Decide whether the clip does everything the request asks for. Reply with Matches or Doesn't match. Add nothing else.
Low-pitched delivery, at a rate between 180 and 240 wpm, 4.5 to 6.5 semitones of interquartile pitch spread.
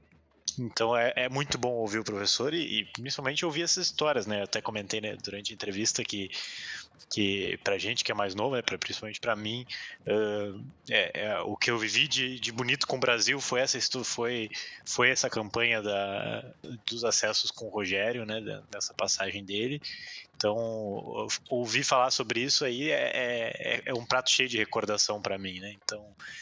Doesn't match